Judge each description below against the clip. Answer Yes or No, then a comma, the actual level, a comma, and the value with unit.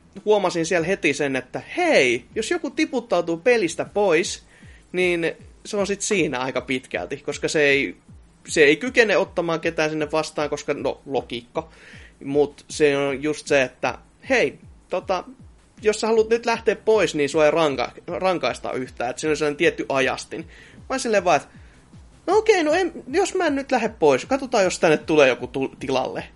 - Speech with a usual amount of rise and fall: No, wide, 8.6 semitones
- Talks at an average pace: No, fast, 175 wpm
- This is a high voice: No, medium, 180 Hz